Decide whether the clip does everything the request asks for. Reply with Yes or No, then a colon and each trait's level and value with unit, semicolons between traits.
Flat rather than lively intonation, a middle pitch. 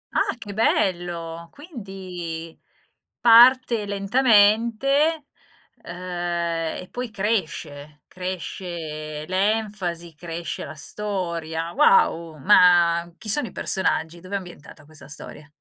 No: average, 4.1 semitones; medium, 180 Hz